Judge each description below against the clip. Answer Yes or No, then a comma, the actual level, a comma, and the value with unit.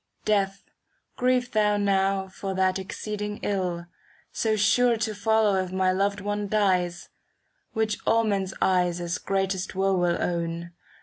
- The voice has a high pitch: Yes, high, 195 Hz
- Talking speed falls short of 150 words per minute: Yes, average, 140 wpm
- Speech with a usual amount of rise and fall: No, narrow, 2.1 semitones